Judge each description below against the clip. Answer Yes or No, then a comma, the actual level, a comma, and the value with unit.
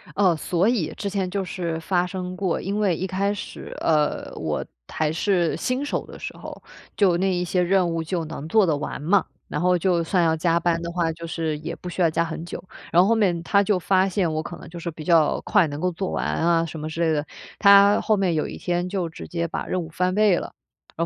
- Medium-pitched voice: Yes, medium, 175 Hz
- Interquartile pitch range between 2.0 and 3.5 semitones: Yes, narrow, 2.5 semitones